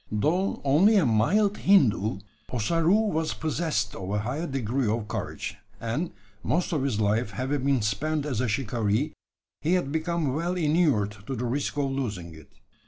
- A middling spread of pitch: No, wide, 6.8 semitones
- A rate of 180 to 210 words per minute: No, average, 170 wpm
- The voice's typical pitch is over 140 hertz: No, low, 135 Hz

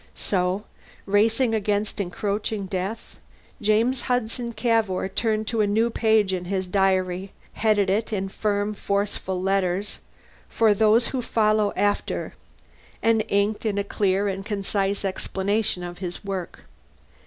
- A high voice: Yes, high, 205 Hz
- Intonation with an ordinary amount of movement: No, narrow, 2.1 semitones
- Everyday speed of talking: No, slow, 130 wpm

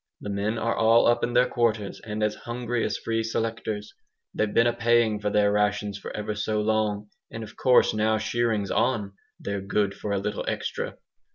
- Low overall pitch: Yes, low, 110 Hz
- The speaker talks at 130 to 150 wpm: No, average, 195 wpm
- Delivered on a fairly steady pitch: Yes, narrow, 1.8 semitones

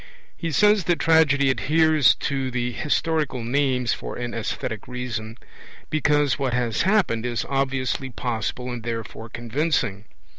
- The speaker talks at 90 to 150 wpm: Yes, slow, 135 wpm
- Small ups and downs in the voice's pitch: No, average, 3.9 semitones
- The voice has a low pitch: Yes, low, 130 Hz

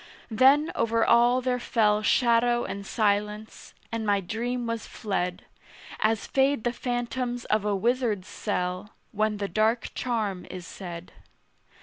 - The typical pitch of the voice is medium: No, high, 220 Hz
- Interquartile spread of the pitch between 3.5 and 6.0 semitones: No, average, 3.0 semitones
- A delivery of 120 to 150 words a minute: Yes, slow, 135 wpm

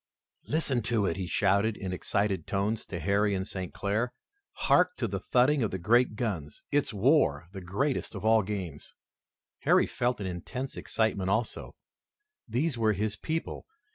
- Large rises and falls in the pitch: No, average, 4.2 semitones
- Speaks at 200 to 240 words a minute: No, average, 165 wpm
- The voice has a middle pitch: No, low, 105 Hz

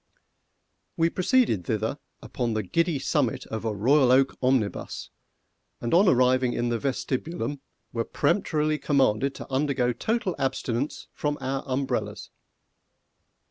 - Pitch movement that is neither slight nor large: Yes, average, 3.8 semitones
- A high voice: No, low, 135 Hz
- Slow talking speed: Yes, slow, 125 wpm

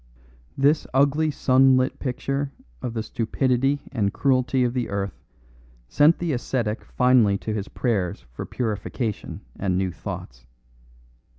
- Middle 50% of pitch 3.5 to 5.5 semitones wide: Yes, average, 4.3 semitones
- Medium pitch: No, low, 125 Hz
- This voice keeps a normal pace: No, slow, 125 wpm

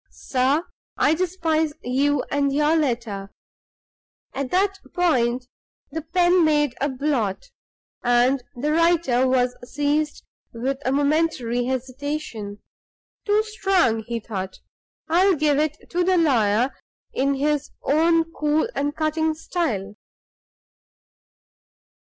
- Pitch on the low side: No, very high, 290 Hz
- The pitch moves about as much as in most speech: Yes, average, 4.5 semitones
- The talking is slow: Yes, slow, 115 wpm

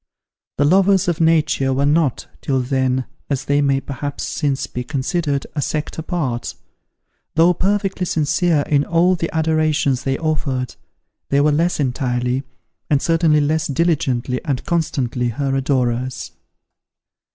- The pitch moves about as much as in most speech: Yes, average, 3.7 semitones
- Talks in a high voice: No, medium, 145 Hz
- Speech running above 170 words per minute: No, slow, 135 wpm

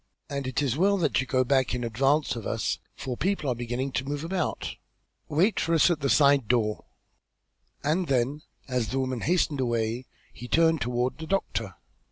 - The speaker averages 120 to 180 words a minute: No, average, 195 wpm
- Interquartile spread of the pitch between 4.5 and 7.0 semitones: No, average, 4.1 semitones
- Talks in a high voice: No, low, 135 Hz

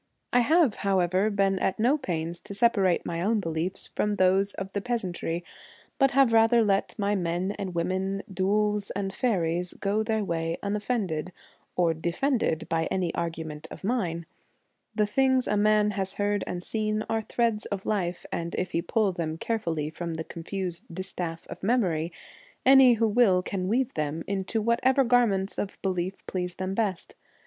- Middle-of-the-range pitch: No, high, 195 Hz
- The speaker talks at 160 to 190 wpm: Yes, average, 175 wpm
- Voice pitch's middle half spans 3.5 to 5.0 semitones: Yes, average, 3.8 semitones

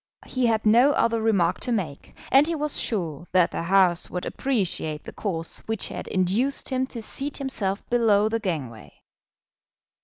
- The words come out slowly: No, average, 165 wpm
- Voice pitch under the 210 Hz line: No, high, 215 Hz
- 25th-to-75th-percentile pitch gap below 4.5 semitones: No, wide, 5.6 semitones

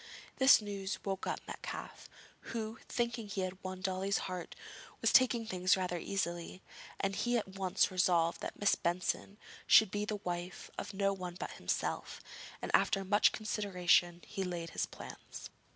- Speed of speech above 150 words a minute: Yes, average, 160 wpm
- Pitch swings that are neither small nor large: No, narrow, 2.3 semitones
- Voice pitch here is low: No, high, 195 Hz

